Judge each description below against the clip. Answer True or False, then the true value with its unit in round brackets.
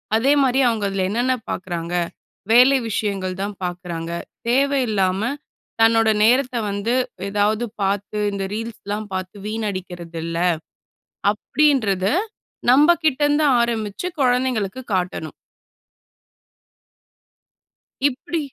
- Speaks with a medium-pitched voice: False (215 Hz)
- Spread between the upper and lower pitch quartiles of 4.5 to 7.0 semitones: True (5.1 semitones)